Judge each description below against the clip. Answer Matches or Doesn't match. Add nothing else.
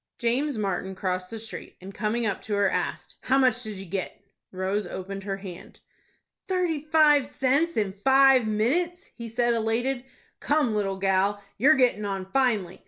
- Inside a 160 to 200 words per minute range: Matches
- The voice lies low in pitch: Doesn't match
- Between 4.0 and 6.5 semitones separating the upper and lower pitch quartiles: Matches